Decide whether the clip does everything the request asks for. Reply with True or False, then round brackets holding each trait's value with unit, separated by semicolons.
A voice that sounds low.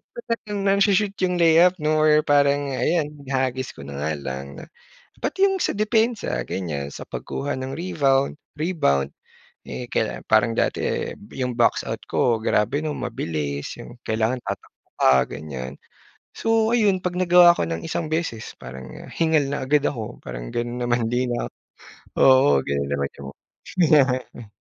True (130 Hz)